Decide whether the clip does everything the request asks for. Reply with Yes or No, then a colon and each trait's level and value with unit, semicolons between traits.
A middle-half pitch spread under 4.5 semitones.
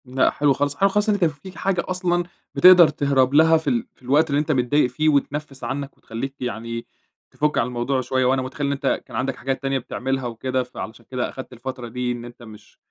Yes: average, 3.3 semitones